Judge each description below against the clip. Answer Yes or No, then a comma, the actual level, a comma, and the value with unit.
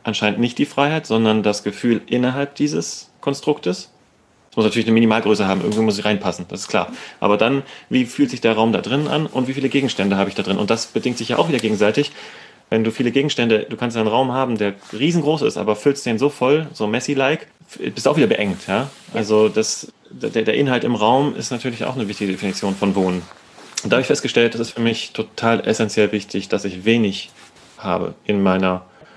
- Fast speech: Yes, fast, 220 wpm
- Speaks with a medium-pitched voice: No, low, 110 Hz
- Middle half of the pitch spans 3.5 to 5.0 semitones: Yes, average, 3.8 semitones